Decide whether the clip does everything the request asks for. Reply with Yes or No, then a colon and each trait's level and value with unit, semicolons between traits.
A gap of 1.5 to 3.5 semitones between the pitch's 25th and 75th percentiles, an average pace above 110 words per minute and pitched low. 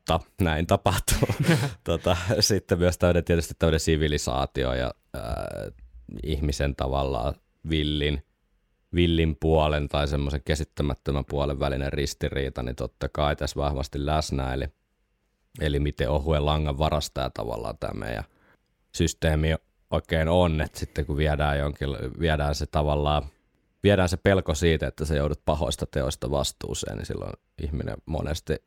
Yes: average, 2.8 semitones; average, 130 wpm; very low, 75 Hz